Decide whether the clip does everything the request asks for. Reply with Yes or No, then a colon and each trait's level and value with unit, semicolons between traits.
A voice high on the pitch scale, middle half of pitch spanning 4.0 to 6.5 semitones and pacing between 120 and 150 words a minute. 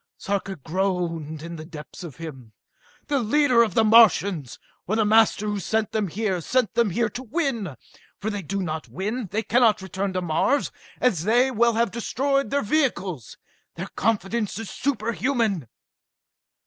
No: high, 210 Hz; average, 4.6 semitones; average, 165 wpm